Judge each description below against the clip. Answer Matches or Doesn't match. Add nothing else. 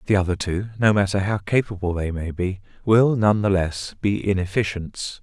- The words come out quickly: Doesn't match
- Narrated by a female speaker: Doesn't match